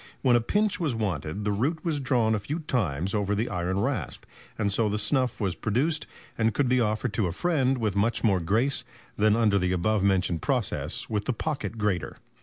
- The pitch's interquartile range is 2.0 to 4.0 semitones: No, average, 4.4 semitones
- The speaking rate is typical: No, fast, 210 wpm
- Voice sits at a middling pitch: No, low, 110 Hz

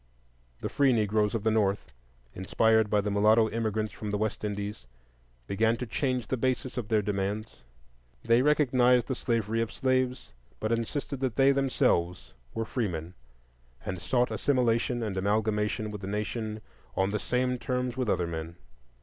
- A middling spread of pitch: Yes, average, 3.4 semitones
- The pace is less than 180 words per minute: Yes, average, 160 wpm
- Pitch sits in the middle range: No, low, 110 Hz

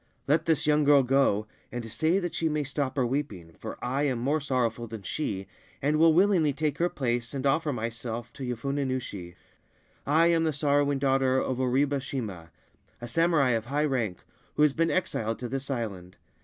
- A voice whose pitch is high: No, low, 135 Hz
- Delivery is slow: No, average, 190 wpm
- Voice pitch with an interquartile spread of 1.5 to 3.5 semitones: No, average, 4.1 semitones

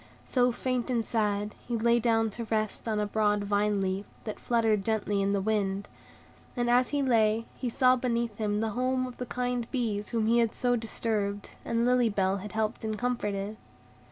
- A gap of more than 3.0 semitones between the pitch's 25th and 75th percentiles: No, narrow, 2.6 semitones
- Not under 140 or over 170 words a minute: No, average, 195 wpm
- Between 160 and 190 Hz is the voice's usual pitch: No, high, 225 Hz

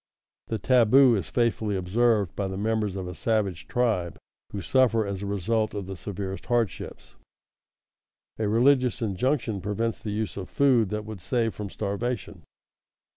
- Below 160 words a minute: Yes, average, 150 wpm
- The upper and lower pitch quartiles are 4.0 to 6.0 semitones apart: No, average, 3.1 semitones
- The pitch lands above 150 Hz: No, low, 105 Hz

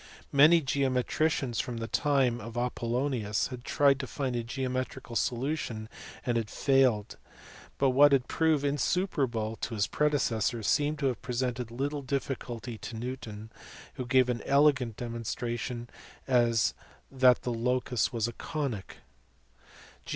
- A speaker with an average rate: No, slow, 130 wpm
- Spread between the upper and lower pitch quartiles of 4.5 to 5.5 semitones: No, average, 2.8 semitones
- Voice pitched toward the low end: Yes, low, 125 Hz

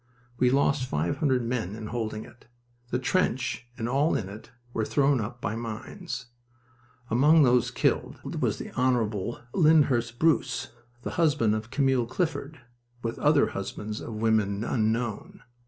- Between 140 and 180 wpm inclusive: Yes, average, 145 wpm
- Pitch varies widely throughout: No, average, 3.8 semitones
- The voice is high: No, low, 120 Hz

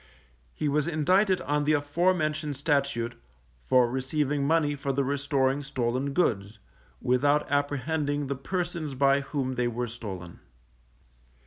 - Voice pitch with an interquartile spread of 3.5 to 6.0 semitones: No, narrow, 2.6 semitones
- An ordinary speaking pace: No, slow, 130 wpm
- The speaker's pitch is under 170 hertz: Yes, medium, 140 Hz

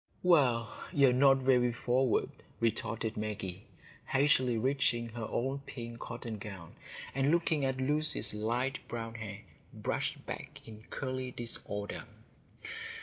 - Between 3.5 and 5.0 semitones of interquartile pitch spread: No, average, 3.1 semitones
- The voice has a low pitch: Yes, low, 120 Hz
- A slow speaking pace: Yes, slow, 125 wpm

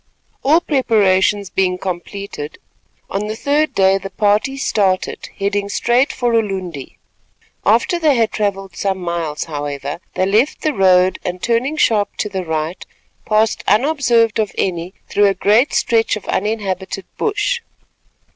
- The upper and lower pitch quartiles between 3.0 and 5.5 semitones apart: Yes, average, 3.8 semitones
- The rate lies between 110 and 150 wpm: Yes, average, 140 wpm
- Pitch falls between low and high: No, high, 200 Hz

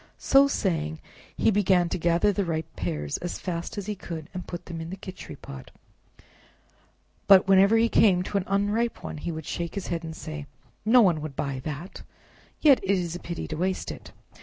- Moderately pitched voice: Yes, medium, 180 Hz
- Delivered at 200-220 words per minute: Yes, fast, 205 wpm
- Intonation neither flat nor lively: Yes, average, 3.7 semitones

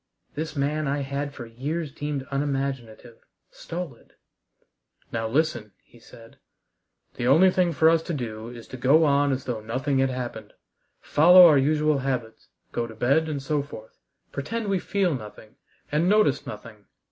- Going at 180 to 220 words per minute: No, average, 160 wpm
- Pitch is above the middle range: No, medium, 140 Hz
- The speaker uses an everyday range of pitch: Yes, average, 4.4 semitones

